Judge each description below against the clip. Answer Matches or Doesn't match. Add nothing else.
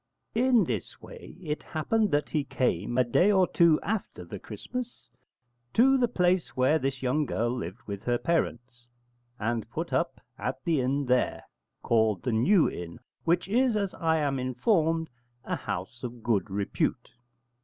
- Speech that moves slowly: Doesn't match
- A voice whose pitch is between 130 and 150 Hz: Matches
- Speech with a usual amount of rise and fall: Doesn't match